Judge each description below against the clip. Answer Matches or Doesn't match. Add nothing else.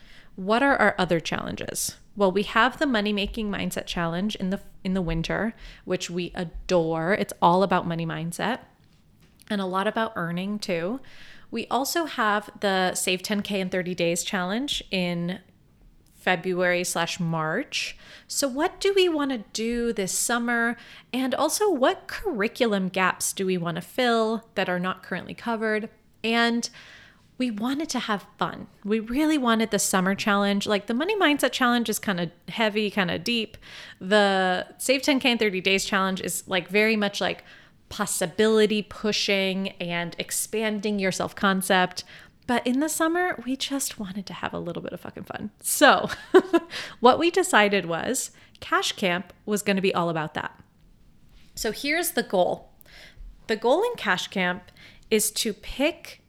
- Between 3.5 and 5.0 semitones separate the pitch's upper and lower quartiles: Matches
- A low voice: Doesn't match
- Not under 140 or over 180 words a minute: Matches